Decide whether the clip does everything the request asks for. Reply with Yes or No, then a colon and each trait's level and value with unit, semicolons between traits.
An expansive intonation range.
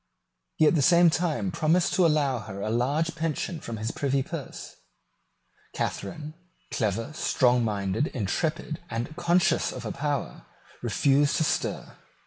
Yes: wide, 5.7 semitones